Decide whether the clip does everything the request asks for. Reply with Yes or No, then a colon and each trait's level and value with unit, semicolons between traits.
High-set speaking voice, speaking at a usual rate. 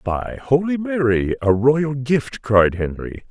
No: low, 130 Hz; average, 145 wpm